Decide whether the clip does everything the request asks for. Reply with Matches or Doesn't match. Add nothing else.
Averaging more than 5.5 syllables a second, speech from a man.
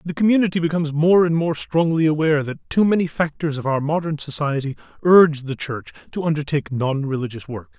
Matches